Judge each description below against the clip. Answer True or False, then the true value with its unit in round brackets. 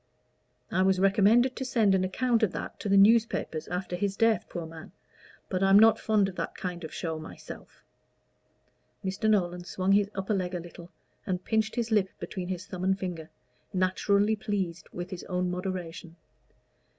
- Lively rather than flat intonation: False (2.5 semitones)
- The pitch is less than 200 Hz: True (190 Hz)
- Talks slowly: False (175 wpm)